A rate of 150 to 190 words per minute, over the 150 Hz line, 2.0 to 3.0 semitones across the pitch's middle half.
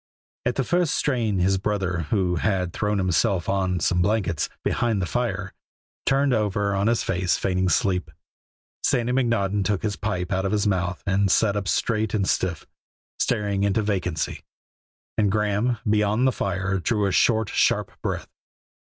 No: average, 160 wpm; low, 100 Hz; average, 2.7 semitones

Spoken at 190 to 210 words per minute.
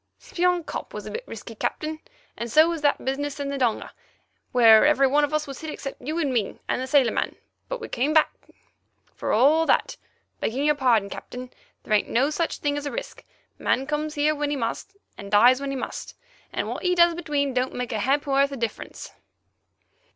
Yes: average, 200 wpm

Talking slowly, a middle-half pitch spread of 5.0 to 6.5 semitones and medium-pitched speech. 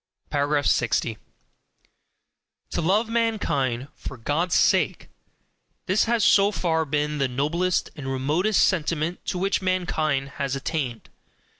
Yes: slow, 115 wpm; average, 5.3 semitones; medium, 160 Hz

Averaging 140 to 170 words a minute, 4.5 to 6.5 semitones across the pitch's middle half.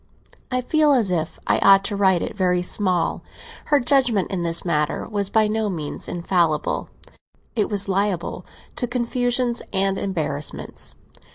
Yes: average, 150 wpm; average, 5.0 semitones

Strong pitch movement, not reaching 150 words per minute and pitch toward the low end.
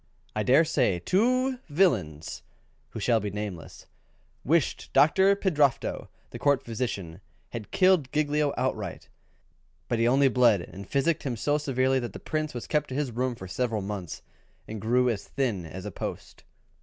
No: wide, 6.0 semitones; average, 170 wpm; low, 125 Hz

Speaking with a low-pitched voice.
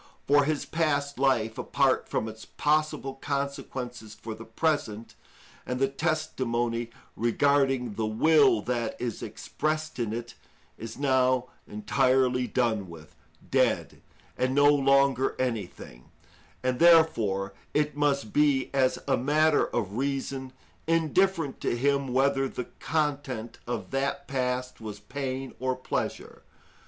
Yes: low, 130 Hz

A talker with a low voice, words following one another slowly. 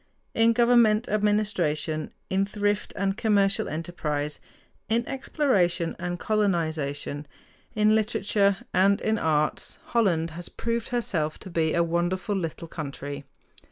No: high, 190 Hz; slow, 120 wpm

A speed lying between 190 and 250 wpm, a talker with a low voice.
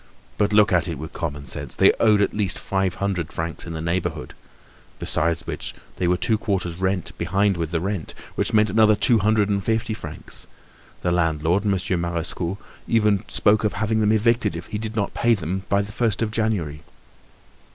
Yes: average, 195 wpm; very low, 95 Hz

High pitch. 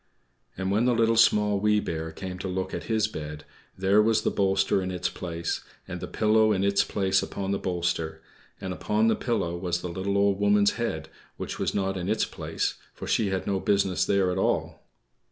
No: very low, 95 Hz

